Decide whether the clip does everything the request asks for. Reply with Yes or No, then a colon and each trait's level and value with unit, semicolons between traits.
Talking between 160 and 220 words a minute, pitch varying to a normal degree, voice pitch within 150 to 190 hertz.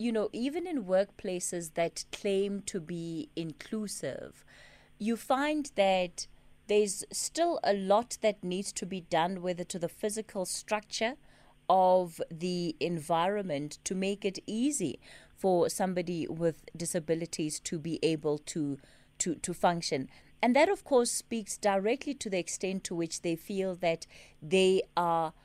No: average, 145 wpm; average, 4.1 semitones; medium, 185 Hz